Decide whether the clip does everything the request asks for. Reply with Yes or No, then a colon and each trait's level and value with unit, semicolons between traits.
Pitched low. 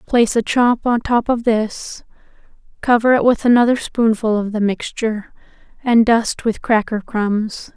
No: high, 225 Hz